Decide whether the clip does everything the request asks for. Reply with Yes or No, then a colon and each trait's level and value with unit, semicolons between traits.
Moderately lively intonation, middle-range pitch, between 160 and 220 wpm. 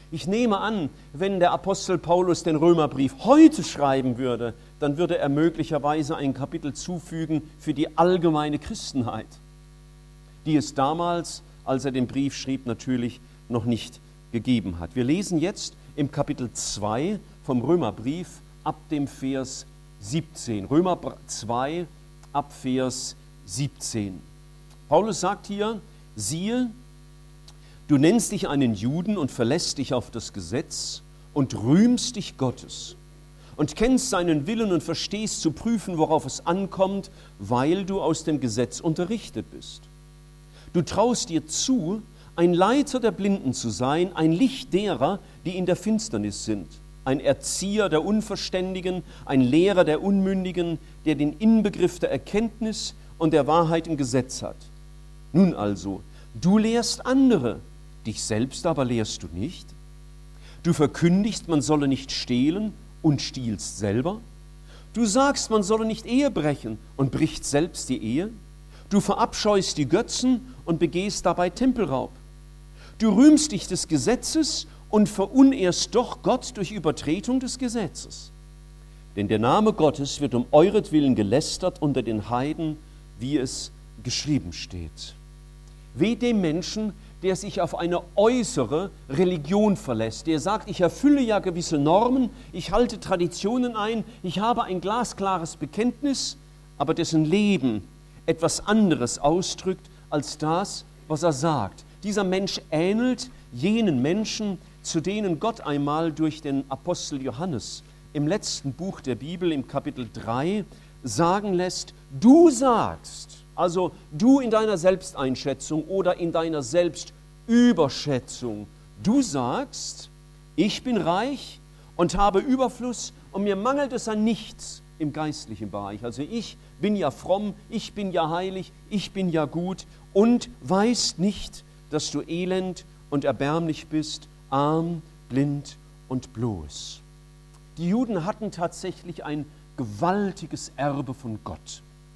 No: average, 4.6 semitones; medium, 155 Hz; average, 135 wpm